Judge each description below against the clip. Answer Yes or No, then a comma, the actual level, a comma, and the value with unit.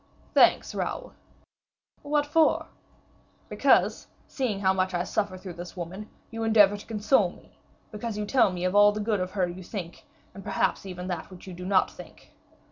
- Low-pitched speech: No, high, 195 Hz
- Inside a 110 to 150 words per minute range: No, average, 180 wpm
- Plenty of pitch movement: No, average, 2.7 semitones